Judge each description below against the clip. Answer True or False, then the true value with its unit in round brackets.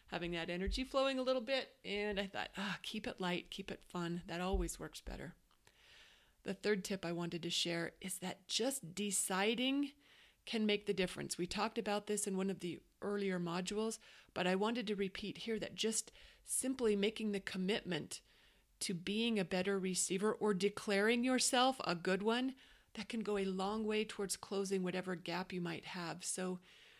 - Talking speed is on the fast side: False (185 wpm)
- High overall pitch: True (200 Hz)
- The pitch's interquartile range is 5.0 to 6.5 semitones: False (3.0 semitones)